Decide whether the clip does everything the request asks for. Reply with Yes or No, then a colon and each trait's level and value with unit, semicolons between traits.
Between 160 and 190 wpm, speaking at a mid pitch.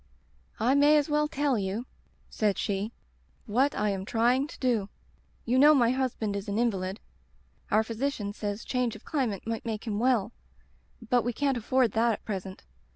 No: average, 175 wpm; high, 230 Hz